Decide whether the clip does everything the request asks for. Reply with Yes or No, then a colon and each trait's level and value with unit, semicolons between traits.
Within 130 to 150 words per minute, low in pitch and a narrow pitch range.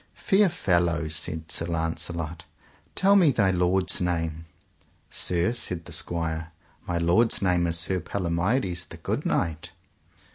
Yes: slow, 135 wpm; very low, 85 Hz; narrow, 2.3 semitones